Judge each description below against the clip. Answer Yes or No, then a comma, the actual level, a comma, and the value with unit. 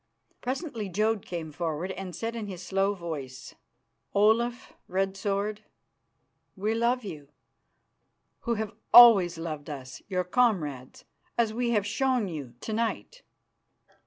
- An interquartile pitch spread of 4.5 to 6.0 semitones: Yes, average, 5.1 semitones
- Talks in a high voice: Yes, high, 200 Hz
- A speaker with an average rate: No, slow, 130 wpm